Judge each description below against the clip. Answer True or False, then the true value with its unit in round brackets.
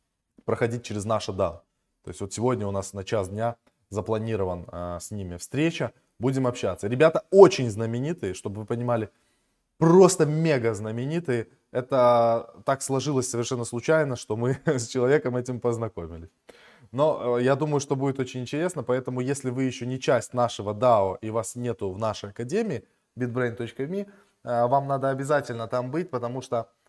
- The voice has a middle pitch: False (120 Hz)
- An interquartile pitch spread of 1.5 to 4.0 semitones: True (3.5 semitones)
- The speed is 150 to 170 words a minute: True (160 wpm)